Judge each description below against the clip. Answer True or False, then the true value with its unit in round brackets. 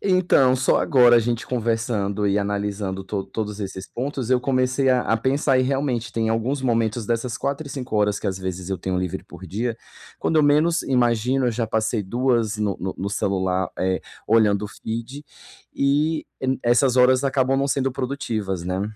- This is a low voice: True (115 Hz)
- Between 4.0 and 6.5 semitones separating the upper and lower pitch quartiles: True (4.3 semitones)